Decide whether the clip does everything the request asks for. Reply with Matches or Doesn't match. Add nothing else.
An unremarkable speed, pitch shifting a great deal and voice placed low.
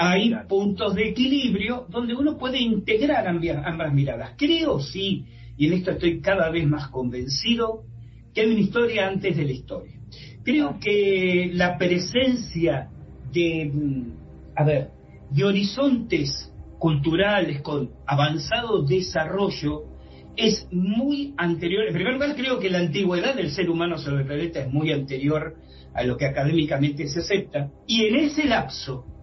Doesn't match